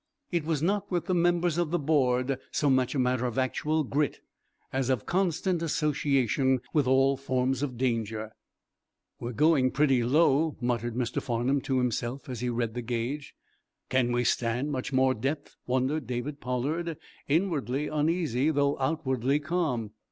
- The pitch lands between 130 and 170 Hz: Yes, low, 135 Hz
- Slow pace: No, average, 160 wpm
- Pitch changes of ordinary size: Yes, average, 3.4 semitones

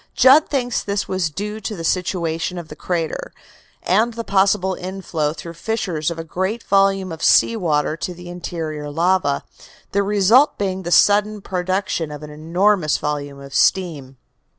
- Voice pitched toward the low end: No, medium, 180 Hz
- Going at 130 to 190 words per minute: Yes, average, 165 wpm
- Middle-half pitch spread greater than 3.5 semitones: Yes, average, 3.9 semitones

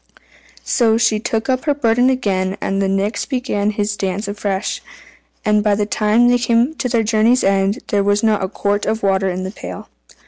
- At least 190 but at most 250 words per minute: Yes, average, 200 wpm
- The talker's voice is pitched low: No, high, 210 Hz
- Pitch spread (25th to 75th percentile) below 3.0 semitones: Yes, narrow, 2.6 semitones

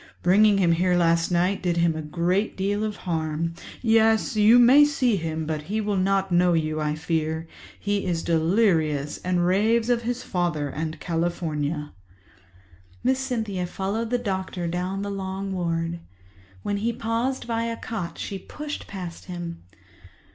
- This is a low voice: No, medium, 185 Hz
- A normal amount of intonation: Yes, average, 4.4 semitones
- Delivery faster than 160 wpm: No, average, 155 wpm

